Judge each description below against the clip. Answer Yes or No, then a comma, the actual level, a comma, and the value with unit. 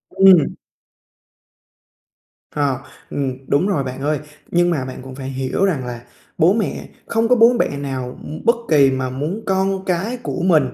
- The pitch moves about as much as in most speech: No, wide, 6.4 semitones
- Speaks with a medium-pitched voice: Yes, medium, 150 Hz